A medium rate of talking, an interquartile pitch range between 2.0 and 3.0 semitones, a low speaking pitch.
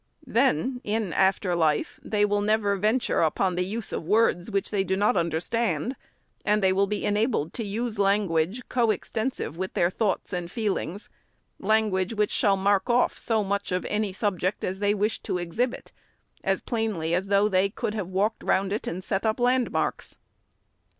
No: average, 185 wpm; average, 2.7 semitones; high, 205 Hz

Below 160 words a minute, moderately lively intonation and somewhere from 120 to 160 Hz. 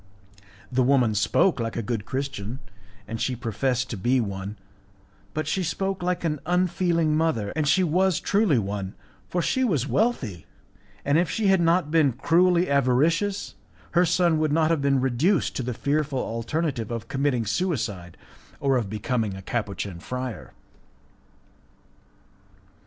No: average, 150 wpm; wide, 6.6 semitones; medium, 140 Hz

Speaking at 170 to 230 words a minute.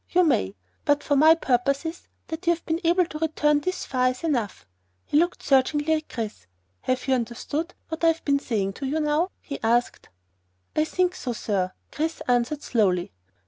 Yes: average, 185 wpm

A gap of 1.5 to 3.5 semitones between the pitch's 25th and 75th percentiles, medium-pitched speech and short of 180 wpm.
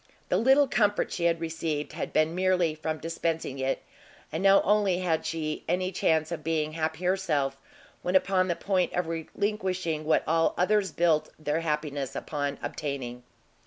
Yes: average, 3.1 semitones; medium, 165 Hz; average, 160 wpm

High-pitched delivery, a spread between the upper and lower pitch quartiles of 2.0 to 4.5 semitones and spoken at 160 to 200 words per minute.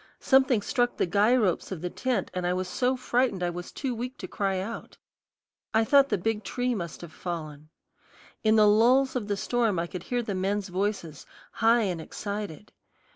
No: high, 205 Hz; average, 5.1 semitones; average, 195 wpm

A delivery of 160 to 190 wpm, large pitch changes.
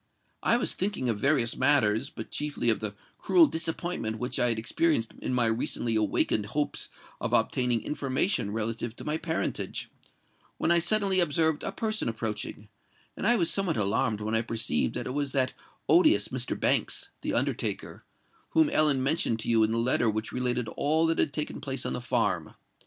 Yes: average, 180 wpm; wide, 6.2 semitones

